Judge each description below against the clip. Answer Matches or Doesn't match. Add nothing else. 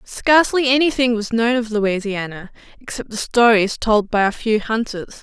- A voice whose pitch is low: Doesn't match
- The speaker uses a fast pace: Doesn't match